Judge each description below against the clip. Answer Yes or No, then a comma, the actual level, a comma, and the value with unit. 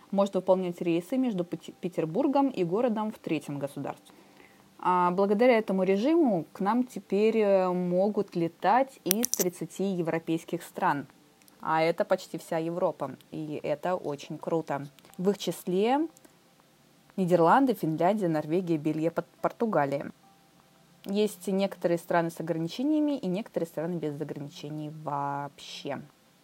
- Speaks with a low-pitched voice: No, medium, 180 Hz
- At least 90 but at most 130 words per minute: Yes, average, 115 wpm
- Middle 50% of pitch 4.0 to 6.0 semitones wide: No, average, 3.4 semitones